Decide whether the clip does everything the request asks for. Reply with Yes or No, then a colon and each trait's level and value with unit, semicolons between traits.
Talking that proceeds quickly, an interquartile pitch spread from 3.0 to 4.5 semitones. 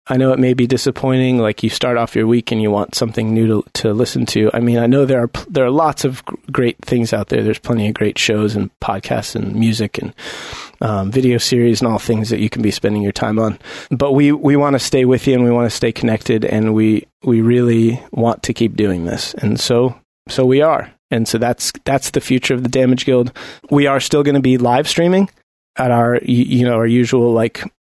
No: fast, 245 wpm; narrow, 2.6 semitones